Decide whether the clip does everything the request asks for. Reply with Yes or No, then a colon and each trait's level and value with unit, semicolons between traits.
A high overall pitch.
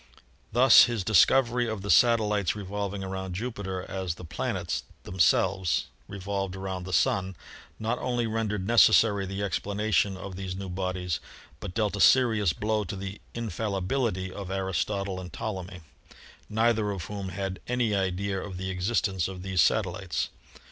No: very low, 95 Hz